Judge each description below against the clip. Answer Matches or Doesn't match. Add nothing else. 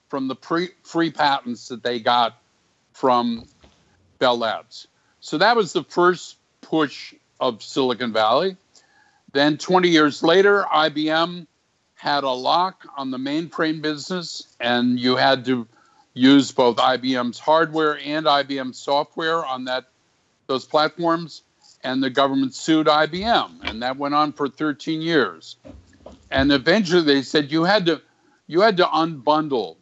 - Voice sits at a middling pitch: Matches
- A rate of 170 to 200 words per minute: Doesn't match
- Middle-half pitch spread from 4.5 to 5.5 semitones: Doesn't match